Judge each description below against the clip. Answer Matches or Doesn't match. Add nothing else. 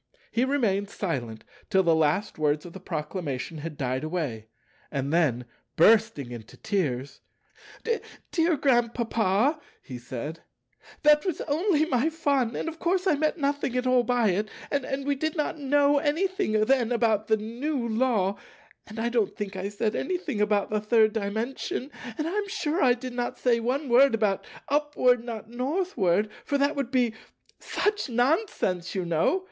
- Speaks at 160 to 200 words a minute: Matches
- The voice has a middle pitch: Doesn't match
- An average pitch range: Doesn't match